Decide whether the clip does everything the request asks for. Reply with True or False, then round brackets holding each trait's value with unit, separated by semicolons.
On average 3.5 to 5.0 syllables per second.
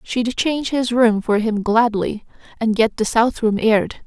True (4.4 syllables/s)